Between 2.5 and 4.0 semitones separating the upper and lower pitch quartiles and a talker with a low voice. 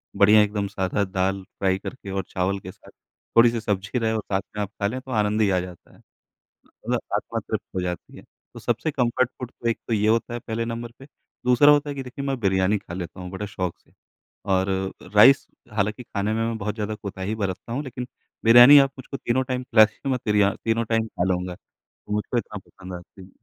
Yes: average, 3.7 semitones; low, 105 Hz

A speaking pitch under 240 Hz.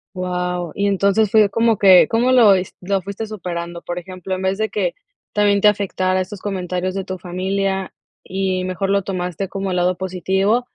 Yes: high, 190 Hz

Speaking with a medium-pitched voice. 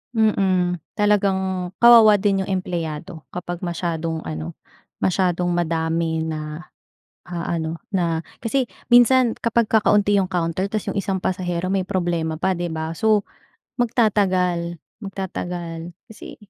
Yes: medium, 180 Hz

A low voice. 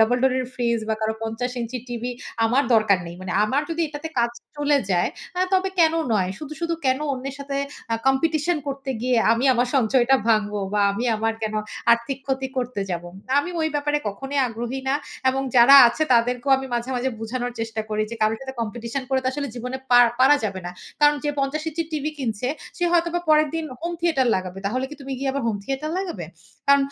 No: very high, 255 Hz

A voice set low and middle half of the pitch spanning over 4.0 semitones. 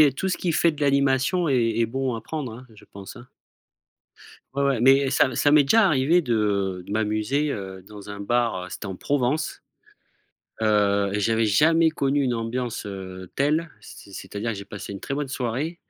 Yes: low, 120 Hz; wide, 5.5 semitones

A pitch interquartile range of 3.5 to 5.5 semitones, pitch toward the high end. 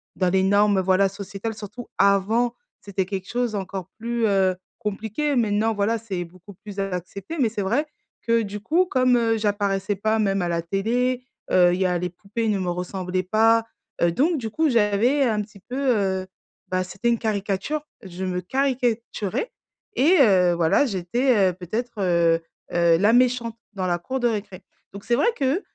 Yes: average, 3.9 semitones; high, 205 Hz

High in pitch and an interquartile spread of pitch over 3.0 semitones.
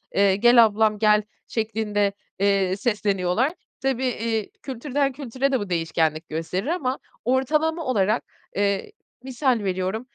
Yes: high, 220 Hz; average, 4.7 semitones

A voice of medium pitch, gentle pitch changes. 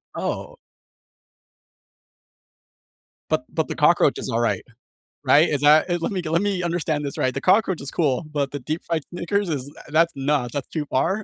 No: medium, 155 Hz; average, 3.7 semitones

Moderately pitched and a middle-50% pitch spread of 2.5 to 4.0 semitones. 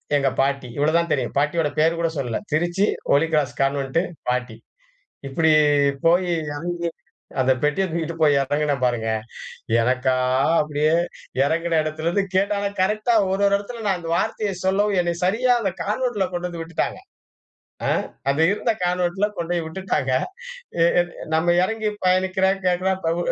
No: medium, 170 Hz; average, 4.4 semitones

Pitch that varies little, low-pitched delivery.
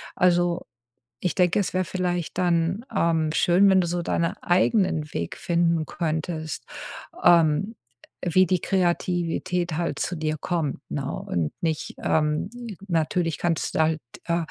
No: narrow, 2.2 semitones; medium, 170 Hz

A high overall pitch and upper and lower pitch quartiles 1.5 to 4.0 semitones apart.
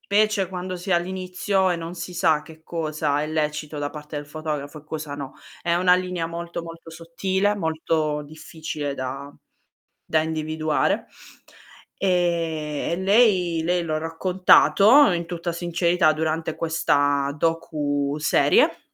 No: medium, 165 Hz; narrow, 2.6 semitones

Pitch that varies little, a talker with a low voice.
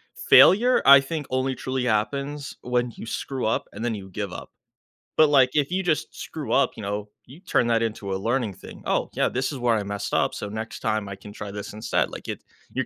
No: average, 4.7 semitones; low, 120 Hz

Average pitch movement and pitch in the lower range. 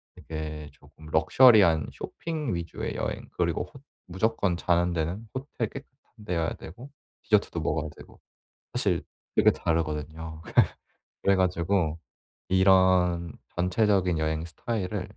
Yes: average, 4.4 semitones; very low, 90 Hz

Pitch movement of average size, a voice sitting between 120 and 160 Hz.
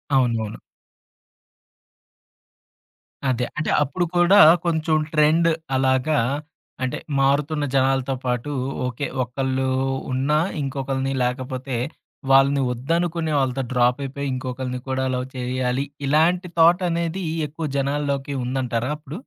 Yes: average, 3.0 semitones; low, 135 Hz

